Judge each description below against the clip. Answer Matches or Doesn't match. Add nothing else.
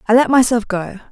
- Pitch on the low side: Doesn't match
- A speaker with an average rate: Doesn't match